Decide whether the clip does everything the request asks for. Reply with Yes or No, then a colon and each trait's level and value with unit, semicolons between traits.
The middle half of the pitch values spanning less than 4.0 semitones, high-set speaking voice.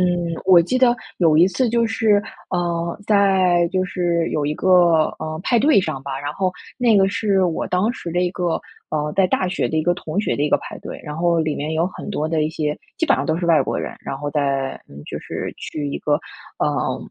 No: average, 3.6 semitones; medium, 175 Hz